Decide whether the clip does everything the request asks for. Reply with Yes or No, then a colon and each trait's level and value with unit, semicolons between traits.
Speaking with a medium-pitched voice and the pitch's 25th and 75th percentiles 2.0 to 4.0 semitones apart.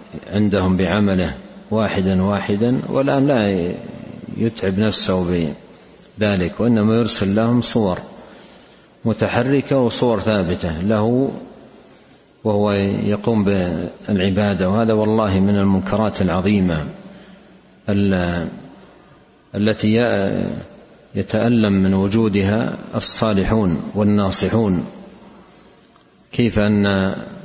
No: low, 105 Hz; average, 2.8 semitones